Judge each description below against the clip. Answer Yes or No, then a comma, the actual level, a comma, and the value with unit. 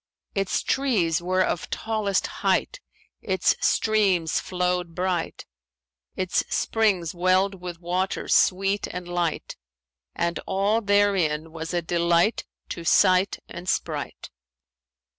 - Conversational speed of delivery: No, slow, 110 wpm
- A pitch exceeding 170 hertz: Yes, medium, 185 Hz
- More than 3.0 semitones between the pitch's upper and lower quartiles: No, narrow, 2.4 semitones